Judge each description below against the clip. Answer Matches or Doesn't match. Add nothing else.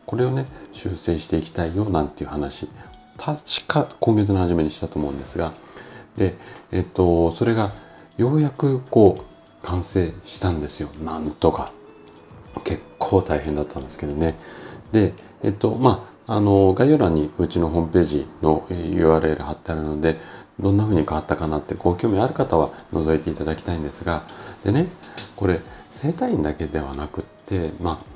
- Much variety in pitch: Doesn't match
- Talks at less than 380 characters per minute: Matches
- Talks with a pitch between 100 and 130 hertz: Doesn't match